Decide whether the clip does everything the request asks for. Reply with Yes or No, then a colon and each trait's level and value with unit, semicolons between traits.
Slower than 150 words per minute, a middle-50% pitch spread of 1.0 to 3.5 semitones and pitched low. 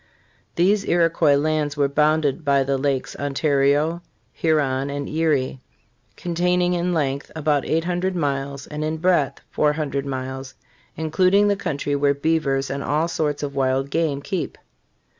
No: average, 140 wpm; average, 2.9 semitones; medium, 150 Hz